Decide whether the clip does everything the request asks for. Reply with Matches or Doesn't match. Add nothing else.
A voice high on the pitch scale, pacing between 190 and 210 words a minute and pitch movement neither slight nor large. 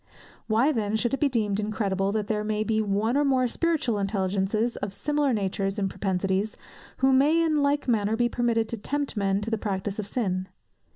Matches